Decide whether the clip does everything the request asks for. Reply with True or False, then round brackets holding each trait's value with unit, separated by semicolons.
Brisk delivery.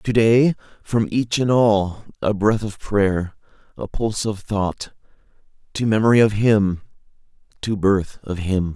False (135 wpm)